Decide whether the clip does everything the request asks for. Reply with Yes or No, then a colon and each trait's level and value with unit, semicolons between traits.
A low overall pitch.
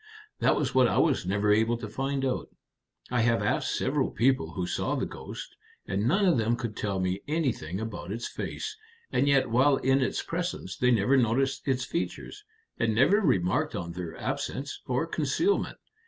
Yes: low, 125 Hz